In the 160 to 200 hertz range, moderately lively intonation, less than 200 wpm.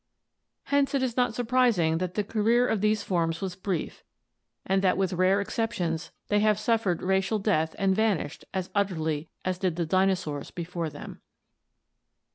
Yes: high, 190 Hz; average, 3.7 semitones; average, 160 wpm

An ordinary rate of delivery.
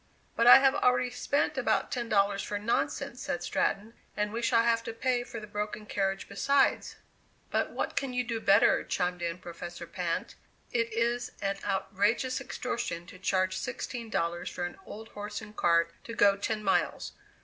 Yes: average, 180 wpm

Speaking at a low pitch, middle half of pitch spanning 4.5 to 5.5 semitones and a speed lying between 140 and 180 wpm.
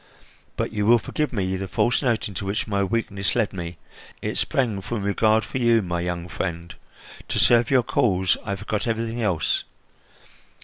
No: low, 105 Hz; average, 3.5 semitones; average, 175 wpm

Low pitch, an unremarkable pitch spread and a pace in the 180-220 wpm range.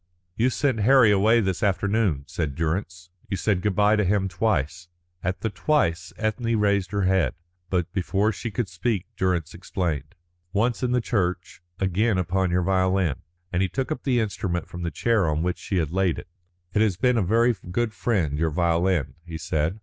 Yes: very low, 95 Hz; average, 3.9 semitones; average, 190 wpm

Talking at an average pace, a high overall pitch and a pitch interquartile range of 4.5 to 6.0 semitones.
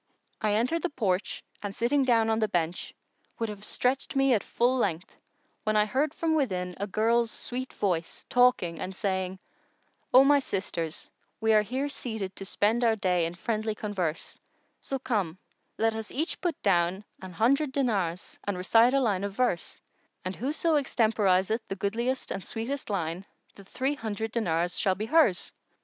Yes: average, 170 wpm; high, 215 Hz; average, 5.0 semitones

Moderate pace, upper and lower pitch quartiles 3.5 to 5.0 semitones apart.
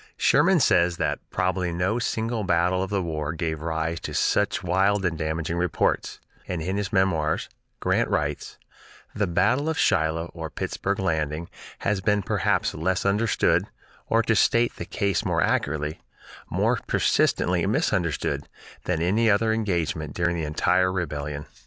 Yes: average, 150 wpm; average, 3.9 semitones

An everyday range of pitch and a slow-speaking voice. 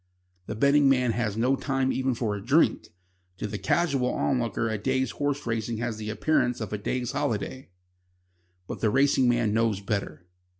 No: average, 3.7 semitones; average, 175 wpm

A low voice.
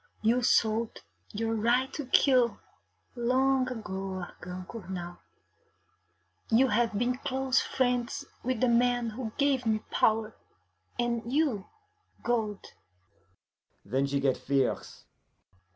No: high, 235 Hz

